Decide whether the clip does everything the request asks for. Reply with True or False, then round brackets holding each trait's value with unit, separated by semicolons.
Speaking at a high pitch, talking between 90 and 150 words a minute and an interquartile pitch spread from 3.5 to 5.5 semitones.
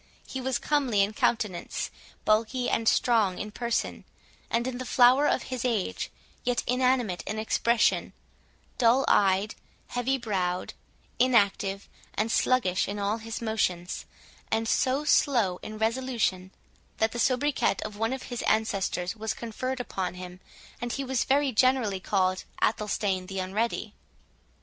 True (225 Hz; 140 wpm; 4.1 semitones)